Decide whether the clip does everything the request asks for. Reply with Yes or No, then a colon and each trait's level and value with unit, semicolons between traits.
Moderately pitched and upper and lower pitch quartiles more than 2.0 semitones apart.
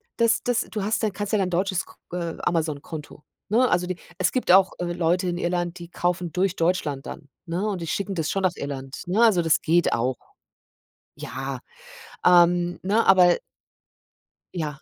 Yes: medium, 175 Hz; average, 2.8 semitones